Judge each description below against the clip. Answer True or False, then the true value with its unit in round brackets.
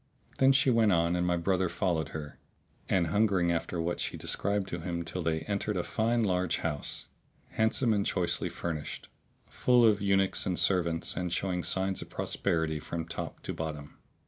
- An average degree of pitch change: True (3.1 semitones)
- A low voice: True (90 Hz)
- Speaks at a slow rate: False (175 wpm)